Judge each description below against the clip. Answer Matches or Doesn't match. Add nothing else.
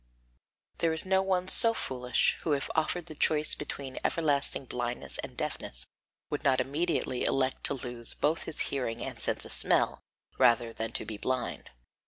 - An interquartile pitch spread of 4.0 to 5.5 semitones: Matches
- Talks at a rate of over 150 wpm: Matches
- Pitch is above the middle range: Doesn't match